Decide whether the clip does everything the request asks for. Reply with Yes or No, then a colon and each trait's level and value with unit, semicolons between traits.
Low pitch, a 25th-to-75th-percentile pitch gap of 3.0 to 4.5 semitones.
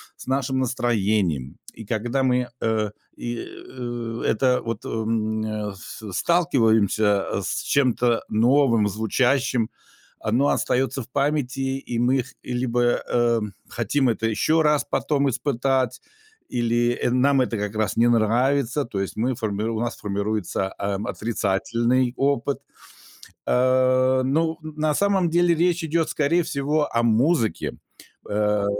Yes: low, 120 Hz; average, 3.6 semitones